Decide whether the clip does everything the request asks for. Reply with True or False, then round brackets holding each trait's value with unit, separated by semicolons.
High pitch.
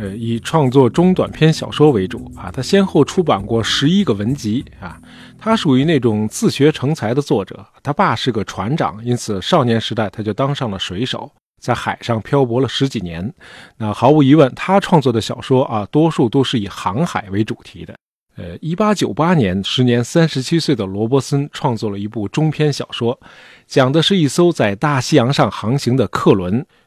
False (130 Hz)